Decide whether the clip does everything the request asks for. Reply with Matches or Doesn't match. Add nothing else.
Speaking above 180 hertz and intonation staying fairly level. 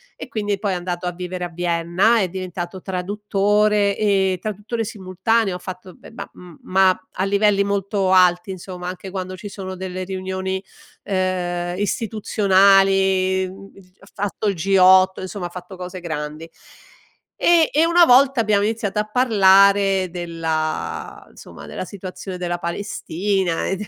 Matches